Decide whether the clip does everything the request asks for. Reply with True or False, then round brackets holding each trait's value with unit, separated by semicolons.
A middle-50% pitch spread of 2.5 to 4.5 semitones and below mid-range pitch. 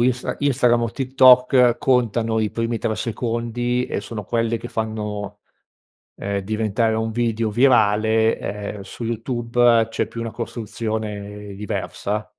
False (2.0 semitones; 115 Hz)